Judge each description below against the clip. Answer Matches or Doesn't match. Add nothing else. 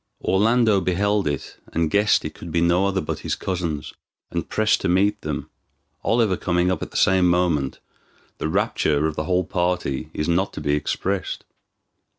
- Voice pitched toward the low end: Matches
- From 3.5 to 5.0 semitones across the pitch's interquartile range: Matches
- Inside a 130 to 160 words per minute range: Doesn't match